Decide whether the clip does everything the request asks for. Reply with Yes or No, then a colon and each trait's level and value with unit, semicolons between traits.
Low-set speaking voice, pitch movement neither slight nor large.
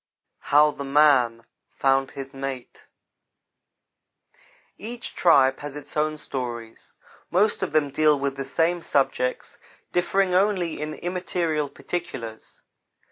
No: medium, 150 Hz; average, 4.2 semitones